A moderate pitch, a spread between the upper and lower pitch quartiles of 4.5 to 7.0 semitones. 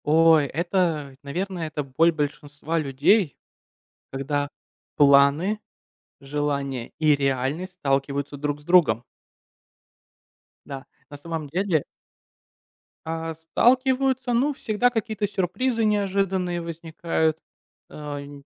Yes: medium, 160 Hz; average, 4.9 semitones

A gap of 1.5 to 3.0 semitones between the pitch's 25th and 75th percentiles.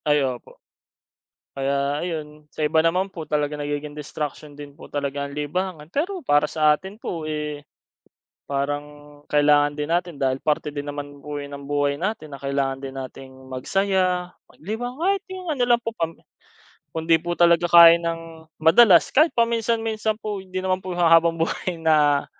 No: average, 4.0 semitones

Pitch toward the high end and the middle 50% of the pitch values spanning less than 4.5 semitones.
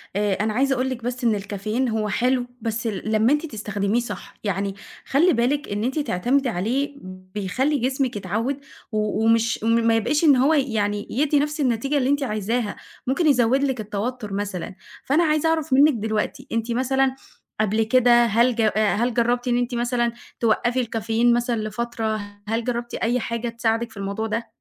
Yes: high, 235 Hz; average, 3.2 semitones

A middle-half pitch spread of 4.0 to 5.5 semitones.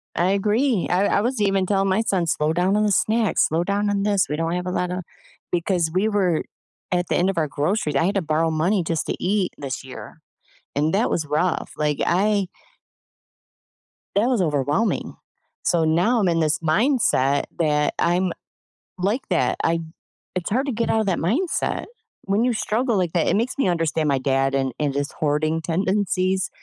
Yes: average, 4.4 semitones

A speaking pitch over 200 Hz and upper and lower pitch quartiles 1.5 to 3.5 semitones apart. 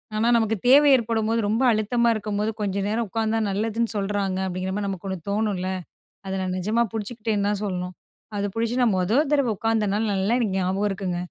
Yes: high, 210 Hz; average, 2.7 semitones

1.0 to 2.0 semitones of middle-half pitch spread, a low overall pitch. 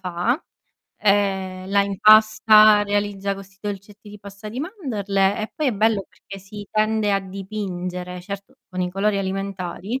No: narrow, 1.7 semitones; high, 200 Hz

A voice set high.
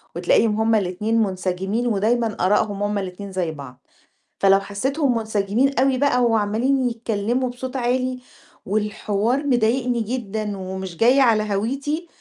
Yes: high, 220 Hz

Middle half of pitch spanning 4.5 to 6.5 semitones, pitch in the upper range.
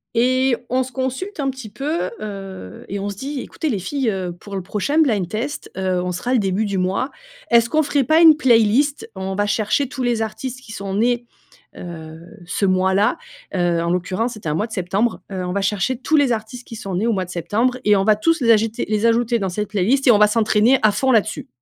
Yes: average, 4.8 semitones; high, 215 Hz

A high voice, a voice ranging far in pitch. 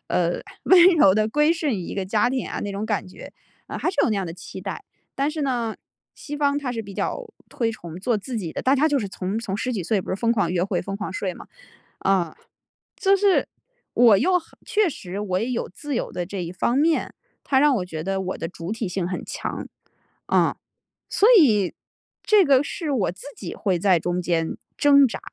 Yes: high, 215 Hz; wide, 7.0 semitones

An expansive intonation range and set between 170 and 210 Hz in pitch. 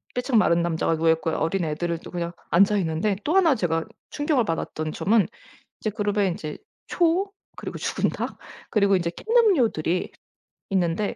Yes: wide, 5.8 semitones; high, 195 Hz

